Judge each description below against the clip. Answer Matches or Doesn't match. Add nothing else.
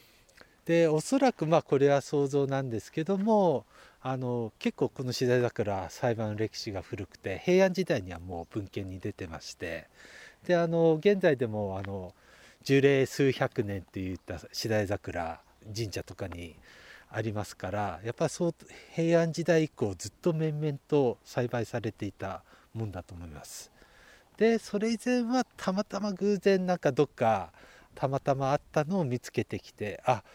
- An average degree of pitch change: Doesn't match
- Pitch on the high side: Doesn't match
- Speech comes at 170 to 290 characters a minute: Doesn't match